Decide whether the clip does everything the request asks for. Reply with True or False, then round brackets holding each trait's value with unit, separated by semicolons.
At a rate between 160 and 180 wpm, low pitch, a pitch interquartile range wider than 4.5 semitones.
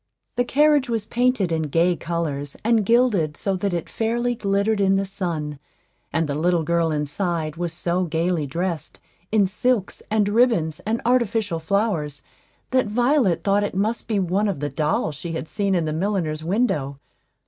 False (170 wpm; 185 Hz; 5.2 semitones)